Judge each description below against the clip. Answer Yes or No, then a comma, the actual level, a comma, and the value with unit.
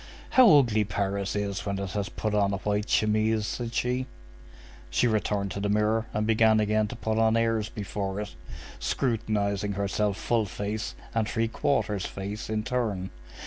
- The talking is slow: No, average, 170 wpm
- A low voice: Yes, low, 105 Hz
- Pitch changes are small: Yes, narrow, 1.8 semitones